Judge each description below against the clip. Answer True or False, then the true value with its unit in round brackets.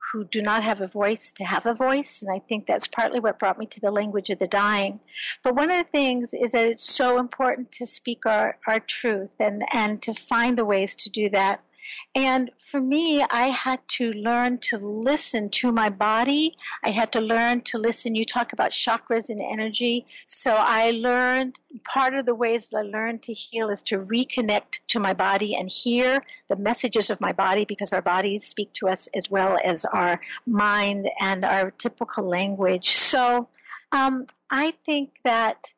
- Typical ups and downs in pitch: True (3.4 semitones)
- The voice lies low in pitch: False (230 Hz)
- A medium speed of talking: True (195 wpm)